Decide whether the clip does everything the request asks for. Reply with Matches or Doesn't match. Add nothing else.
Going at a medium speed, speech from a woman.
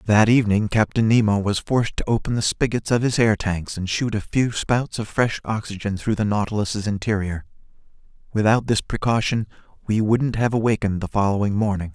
Doesn't match